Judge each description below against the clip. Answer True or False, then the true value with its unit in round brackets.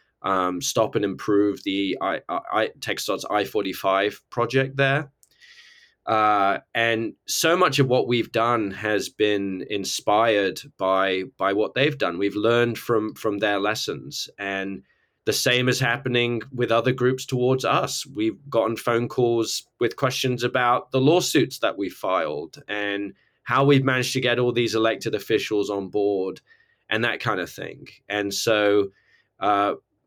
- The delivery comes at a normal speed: True (150 wpm)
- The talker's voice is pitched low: True (115 Hz)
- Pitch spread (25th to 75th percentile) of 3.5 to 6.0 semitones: True (4.0 semitones)